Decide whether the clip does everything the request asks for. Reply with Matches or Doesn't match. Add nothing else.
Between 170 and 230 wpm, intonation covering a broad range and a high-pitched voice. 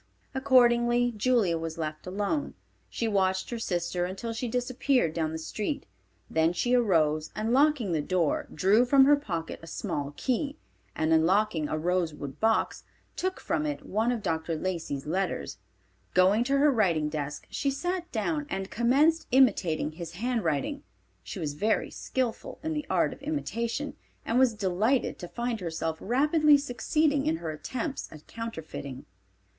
Doesn't match